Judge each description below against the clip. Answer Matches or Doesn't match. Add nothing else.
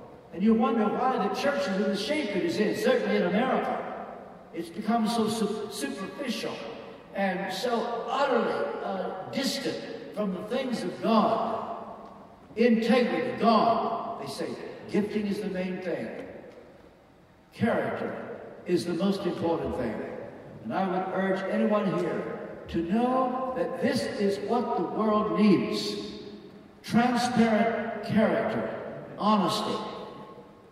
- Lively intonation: Doesn't match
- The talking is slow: Matches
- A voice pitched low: Doesn't match